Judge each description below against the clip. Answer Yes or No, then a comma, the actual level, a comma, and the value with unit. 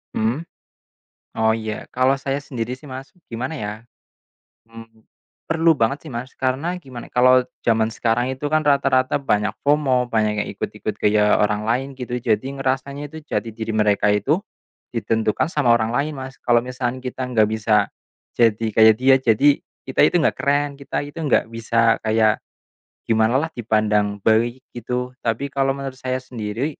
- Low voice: Yes, low, 125 Hz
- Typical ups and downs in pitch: Yes, average, 3.4 semitones